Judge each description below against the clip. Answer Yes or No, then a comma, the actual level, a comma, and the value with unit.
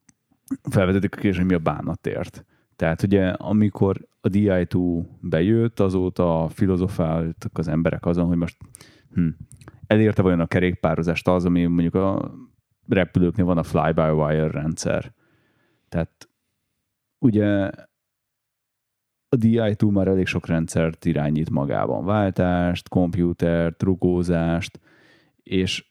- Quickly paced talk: No, average, 115 wpm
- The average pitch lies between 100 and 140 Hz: No, very low, 90 Hz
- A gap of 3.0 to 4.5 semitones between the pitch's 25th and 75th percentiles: Yes, average, 3.4 semitones